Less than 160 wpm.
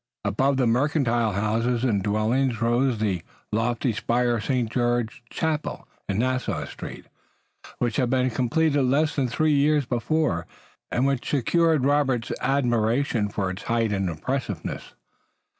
Yes: average, 140 wpm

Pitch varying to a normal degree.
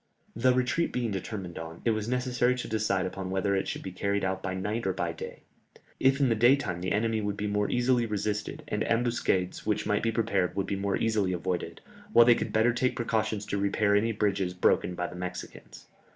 Yes: average, 3.4 semitones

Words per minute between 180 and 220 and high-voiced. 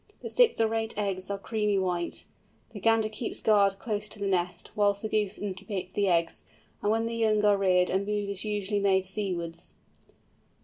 Yes: average, 190 wpm; high, 200 Hz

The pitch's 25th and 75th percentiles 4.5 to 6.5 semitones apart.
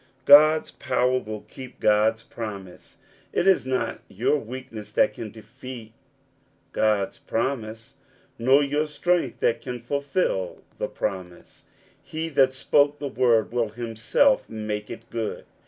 No: average, 4.1 semitones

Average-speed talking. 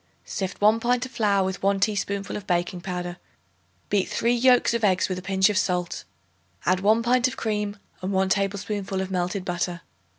Yes: average, 190 wpm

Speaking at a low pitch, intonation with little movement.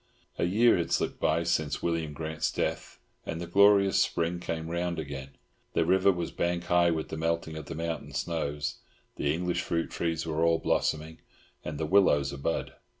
Yes: very low, 85 Hz; narrow, 1.8 semitones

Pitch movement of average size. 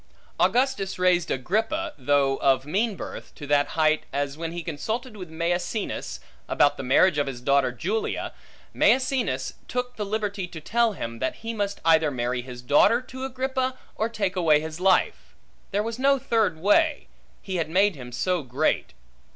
No: wide, 7.5 semitones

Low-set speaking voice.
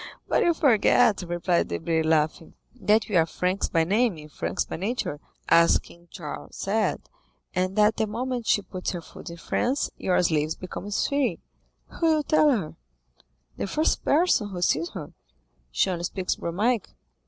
No: high, 190 Hz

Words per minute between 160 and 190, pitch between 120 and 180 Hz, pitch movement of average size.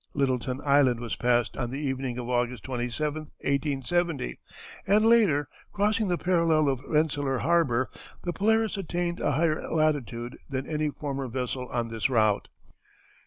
No: average, 145 wpm; medium, 140 Hz; average, 4.9 semitones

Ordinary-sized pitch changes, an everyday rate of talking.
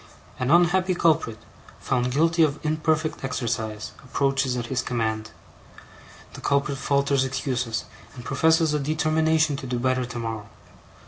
No: average, 4.1 semitones; slow, 130 wpm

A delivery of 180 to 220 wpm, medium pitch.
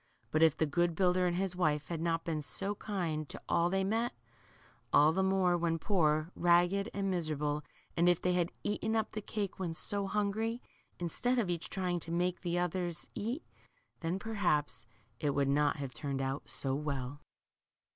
Yes: average, 185 wpm; medium, 175 Hz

